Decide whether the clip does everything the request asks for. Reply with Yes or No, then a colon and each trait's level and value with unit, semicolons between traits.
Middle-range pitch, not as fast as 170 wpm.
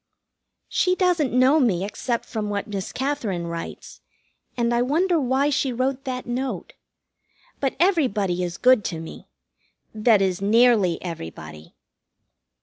No: high, 240 Hz; slow, 135 wpm